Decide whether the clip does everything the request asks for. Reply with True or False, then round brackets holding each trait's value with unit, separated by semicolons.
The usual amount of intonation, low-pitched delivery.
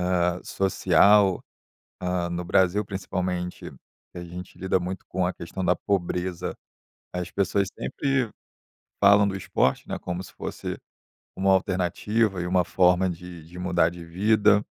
False (1.7 semitones; 90 Hz)